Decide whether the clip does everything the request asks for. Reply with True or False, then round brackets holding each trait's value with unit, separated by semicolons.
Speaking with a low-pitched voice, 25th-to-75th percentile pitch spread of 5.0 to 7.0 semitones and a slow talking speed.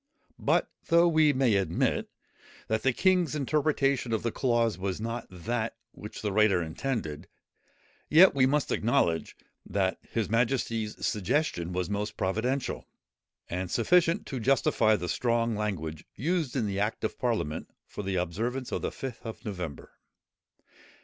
False (115 Hz; 5.4 semitones; 145 wpm)